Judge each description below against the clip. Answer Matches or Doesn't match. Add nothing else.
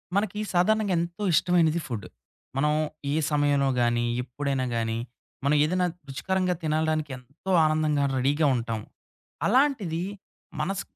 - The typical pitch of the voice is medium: Matches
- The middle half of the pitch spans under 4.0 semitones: Doesn't match